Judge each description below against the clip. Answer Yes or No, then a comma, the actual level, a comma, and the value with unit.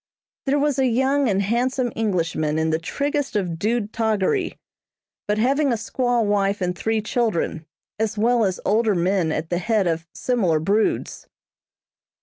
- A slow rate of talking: No, average, 155 wpm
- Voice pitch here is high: Yes, high, 215 Hz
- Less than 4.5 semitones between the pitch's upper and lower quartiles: No, average, 5.1 semitones